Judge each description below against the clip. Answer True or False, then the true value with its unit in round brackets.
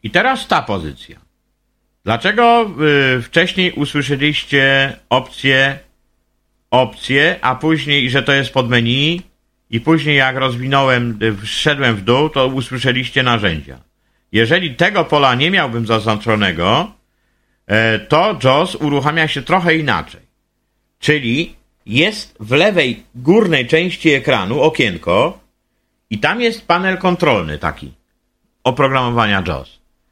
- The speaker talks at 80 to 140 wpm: True (110 wpm)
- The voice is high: False (135 Hz)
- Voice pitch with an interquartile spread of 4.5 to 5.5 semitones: True (5.2 semitones)